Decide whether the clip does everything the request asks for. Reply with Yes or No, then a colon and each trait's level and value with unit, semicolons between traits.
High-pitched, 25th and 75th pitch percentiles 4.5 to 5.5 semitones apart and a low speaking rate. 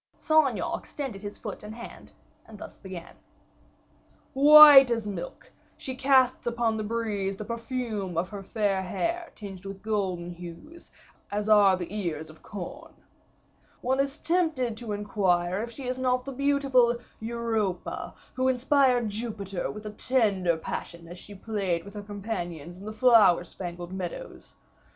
No: high, 215 Hz; average, 5.0 semitones; average, 155 wpm